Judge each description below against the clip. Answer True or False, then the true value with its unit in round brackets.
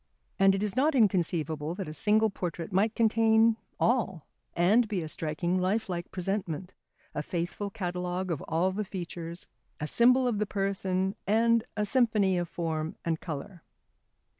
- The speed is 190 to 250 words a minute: False (155 wpm)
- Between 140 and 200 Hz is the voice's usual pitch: True (190 Hz)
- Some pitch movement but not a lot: True (3.9 semitones)